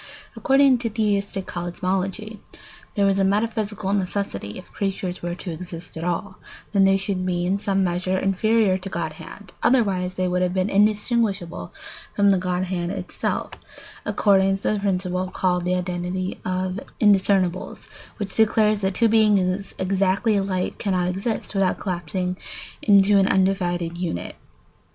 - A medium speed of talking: Yes, average, 145 wpm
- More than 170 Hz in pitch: Yes, high, 190 Hz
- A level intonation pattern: Yes, narrow, 1.8 semitones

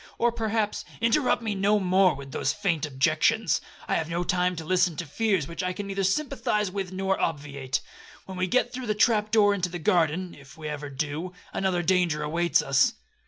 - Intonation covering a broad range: No, average, 4.5 semitones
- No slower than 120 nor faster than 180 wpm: No, average, 200 wpm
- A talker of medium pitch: Yes, medium, 180 Hz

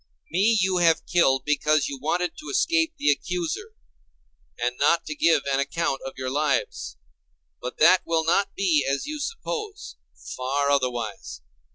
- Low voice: No, medium, 160 Hz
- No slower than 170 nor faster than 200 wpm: No, average, 155 wpm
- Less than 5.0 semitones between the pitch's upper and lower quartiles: No, wide, 5.4 semitones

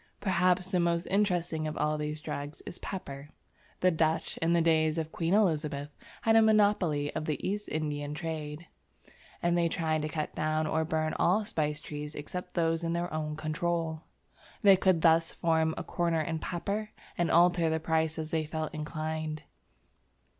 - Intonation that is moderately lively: No, narrow, 2.0 semitones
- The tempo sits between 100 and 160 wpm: No, average, 175 wpm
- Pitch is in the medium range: Yes, medium, 160 Hz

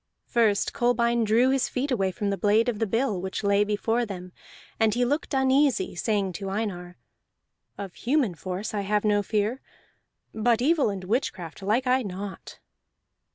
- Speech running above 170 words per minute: No, average, 165 wpm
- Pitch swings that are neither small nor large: Yes, average, 3.6 semitones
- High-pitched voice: Yes, high, 215 Hz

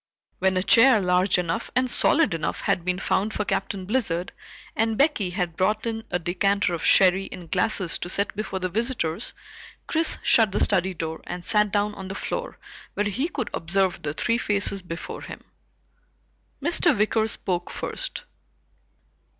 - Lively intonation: No, average, 3.5 semitones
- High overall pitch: Yes, high, 195 Hz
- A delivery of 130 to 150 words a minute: No, average, 165 wpm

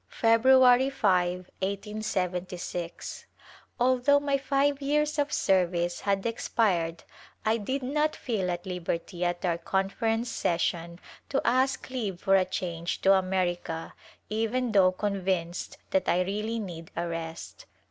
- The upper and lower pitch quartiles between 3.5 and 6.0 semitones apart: Yes, wide, 5.6 semitones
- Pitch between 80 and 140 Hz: No, high, 195 Hz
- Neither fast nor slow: No, slow, 125 wpm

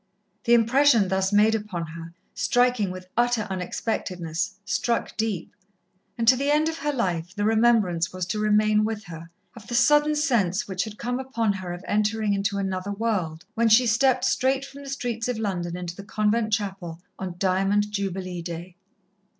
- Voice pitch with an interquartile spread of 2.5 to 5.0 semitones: Yes, average, 4.3 semitones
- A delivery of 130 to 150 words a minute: No, average, 175 wpm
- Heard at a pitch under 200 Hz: No, high, 210 Hz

